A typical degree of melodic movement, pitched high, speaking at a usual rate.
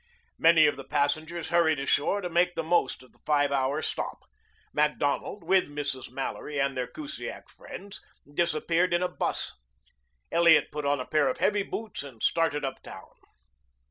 No: average, 3.4 semitones; medium, 155 Hz; average, 165 wpm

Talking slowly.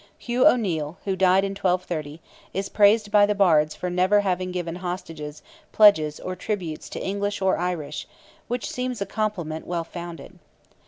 No: average, 160 wpm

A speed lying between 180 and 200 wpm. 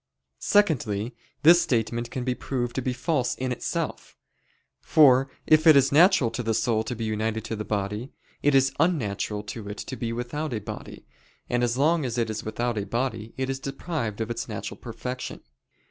Yes: average, 190 wpm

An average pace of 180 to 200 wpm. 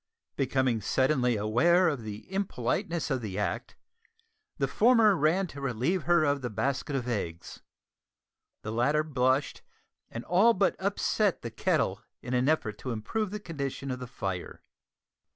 No: average, 150 wpm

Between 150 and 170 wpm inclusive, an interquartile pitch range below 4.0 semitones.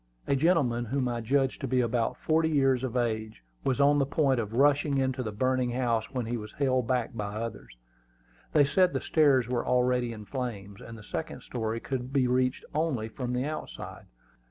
No: average, 200 wpm; average, 2.9 semitones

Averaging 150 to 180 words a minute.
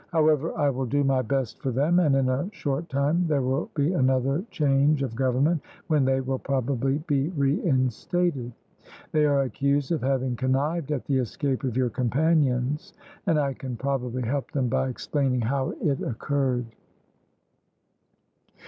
Yes: average, 155 wpm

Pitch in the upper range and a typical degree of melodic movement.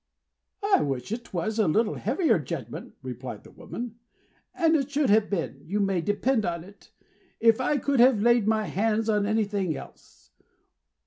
Yes: high, 215 Hz; average, 3.4 semitones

